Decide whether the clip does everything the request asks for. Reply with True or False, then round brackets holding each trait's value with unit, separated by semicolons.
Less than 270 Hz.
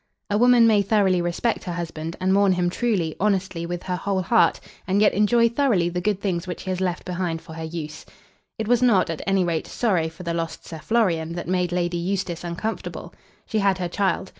True (185 Hz)